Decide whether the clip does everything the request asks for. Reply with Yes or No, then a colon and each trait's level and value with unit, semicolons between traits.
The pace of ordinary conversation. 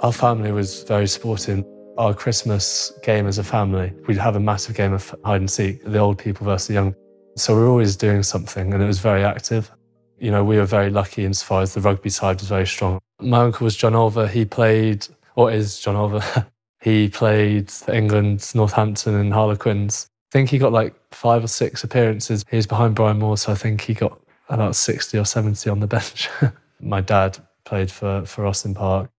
No: fast, 210 wpm